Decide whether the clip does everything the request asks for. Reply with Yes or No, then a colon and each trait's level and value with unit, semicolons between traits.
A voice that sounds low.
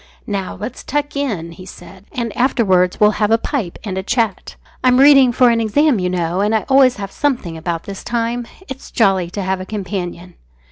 No: high, 210 Hz